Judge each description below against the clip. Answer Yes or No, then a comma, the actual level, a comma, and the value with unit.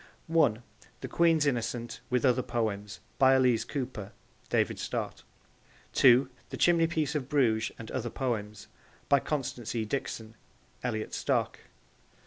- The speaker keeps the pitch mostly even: No, average, 3.7 semitones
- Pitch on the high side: No, low, 125 Hz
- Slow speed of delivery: Yes, slow, 125 wpm